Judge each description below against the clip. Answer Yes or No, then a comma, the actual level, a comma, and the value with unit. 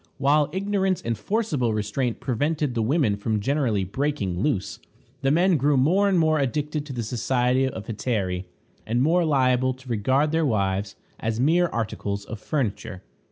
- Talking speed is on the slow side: No, average, 160 wpm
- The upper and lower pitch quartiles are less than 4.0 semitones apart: No, wide, 5.6 semitones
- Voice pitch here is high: No, low, 130 Hz